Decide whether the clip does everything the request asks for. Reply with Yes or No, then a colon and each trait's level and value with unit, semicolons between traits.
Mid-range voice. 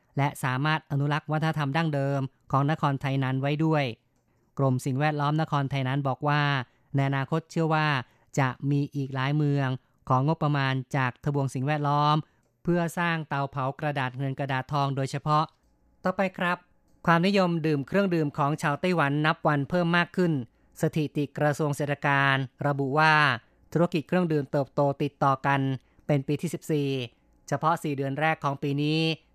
Yes: medium, 145 Hz